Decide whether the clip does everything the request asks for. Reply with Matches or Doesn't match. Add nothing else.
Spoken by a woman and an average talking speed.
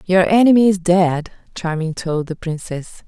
Matches